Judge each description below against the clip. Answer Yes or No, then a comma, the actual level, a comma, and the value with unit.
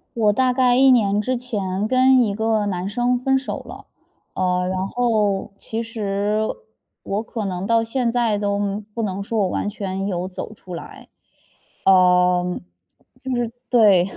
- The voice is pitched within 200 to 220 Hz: Yes, high, 210 Hz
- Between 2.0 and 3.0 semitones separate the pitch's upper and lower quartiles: No, average, 3.4 semitones